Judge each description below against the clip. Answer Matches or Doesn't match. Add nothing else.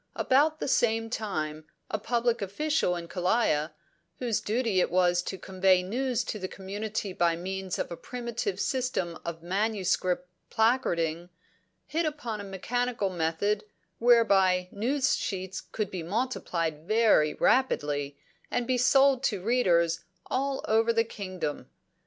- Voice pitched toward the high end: Matches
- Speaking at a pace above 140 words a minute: Doesn't match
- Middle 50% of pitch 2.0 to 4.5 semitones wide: Doesn't match